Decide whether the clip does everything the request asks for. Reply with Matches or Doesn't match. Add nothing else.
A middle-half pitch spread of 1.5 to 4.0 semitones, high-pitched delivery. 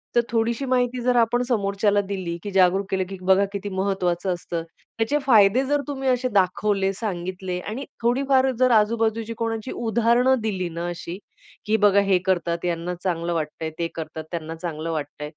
Doesn't match